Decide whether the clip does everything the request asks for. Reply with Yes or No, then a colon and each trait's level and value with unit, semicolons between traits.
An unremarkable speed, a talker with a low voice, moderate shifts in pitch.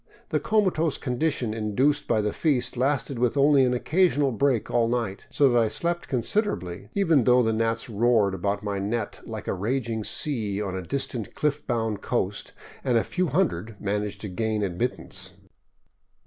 Yes: average, 175 wpm; low, 120 Hz; average, 5.0 semitones